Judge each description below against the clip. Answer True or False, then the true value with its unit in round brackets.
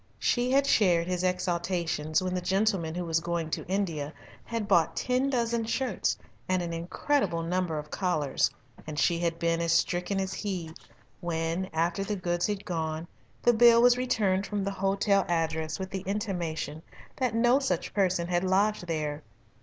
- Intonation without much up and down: False (3.5 semitones)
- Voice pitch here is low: False (180 Hz)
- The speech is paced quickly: False (170 wpm)